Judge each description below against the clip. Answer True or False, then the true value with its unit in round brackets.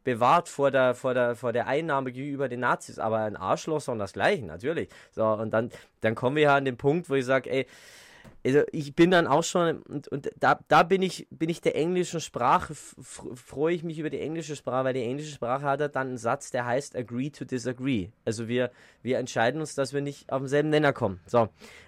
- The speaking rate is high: True (235 wpm)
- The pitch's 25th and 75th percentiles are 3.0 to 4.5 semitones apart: True (3.7 semitones)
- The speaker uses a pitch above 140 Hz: False (135 Hz)